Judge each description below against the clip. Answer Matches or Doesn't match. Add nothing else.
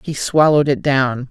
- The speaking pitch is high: Doesn't match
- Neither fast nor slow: Matches